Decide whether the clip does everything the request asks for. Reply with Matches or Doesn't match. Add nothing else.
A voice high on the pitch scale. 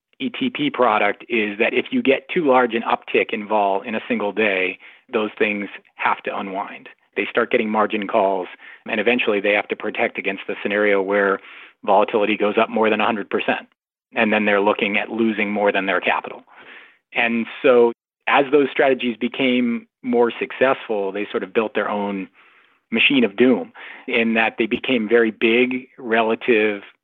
Doesn't match